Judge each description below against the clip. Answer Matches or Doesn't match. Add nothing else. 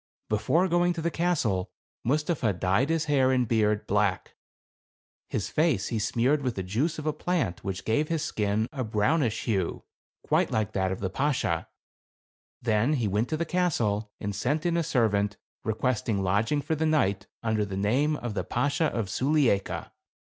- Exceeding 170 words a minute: Matches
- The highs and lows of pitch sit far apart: Matches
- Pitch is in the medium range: Doesn't match